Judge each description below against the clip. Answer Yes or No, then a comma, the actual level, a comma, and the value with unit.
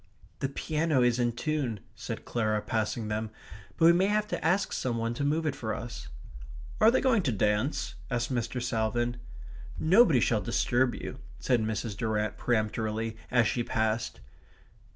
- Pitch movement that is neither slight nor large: Yes, average, 4.7 semitones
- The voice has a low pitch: Yes, low, 120 Hz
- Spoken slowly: No, average, 165 wpm